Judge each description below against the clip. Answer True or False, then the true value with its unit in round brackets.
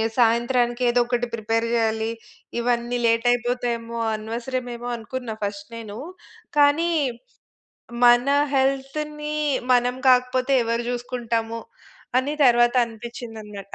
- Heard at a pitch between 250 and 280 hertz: False (240 Hz)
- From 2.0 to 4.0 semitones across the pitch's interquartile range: False (1.6 semitones)